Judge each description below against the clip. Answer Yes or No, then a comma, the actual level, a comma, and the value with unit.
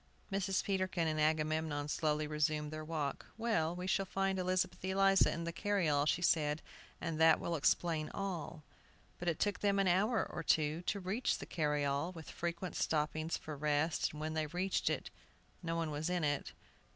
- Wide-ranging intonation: No, average, 3.3 semitones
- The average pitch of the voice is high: No, medium, 165 Hz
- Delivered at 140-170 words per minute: No, average, 180 wpm